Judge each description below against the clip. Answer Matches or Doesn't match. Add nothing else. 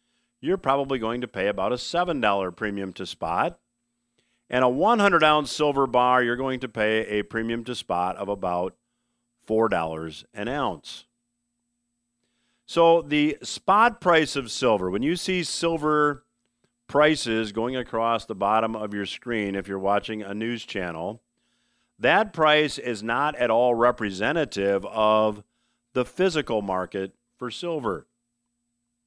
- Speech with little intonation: Doesn't match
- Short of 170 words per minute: Matches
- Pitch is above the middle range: Doesn't match